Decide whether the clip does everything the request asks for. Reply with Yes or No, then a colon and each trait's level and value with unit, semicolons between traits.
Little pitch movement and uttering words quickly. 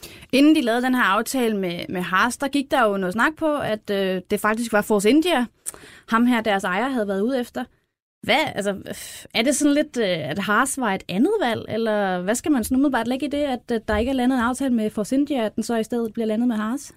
No: average, 4.1 semitones; fast, 250 wpm